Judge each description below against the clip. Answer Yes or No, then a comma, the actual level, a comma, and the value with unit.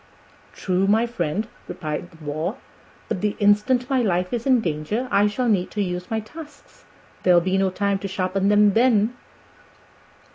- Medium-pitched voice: No, high, 200 Hz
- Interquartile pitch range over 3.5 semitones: Yes, average, 3.9 semitones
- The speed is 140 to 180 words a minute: Yes, average, 170 wpm